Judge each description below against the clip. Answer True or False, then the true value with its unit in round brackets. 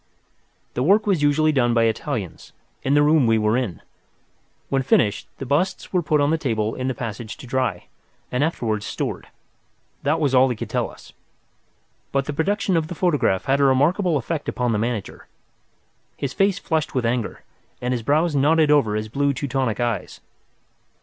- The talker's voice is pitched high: False (135 Hz)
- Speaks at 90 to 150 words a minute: False (185 wpm)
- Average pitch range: True (4.8 semitones)